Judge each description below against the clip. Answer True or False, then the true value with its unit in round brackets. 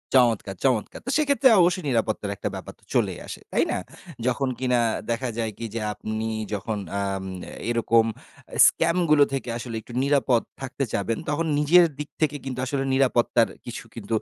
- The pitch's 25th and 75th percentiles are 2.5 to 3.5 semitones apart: False (4.3 semitones)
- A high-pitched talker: False (125 Hz)